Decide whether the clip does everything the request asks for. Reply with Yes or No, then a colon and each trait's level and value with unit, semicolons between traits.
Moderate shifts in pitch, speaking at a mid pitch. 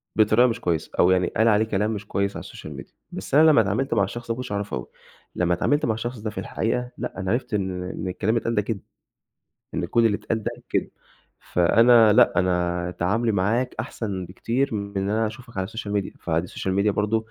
No: average, 3.5 semitones; low, 105 Hz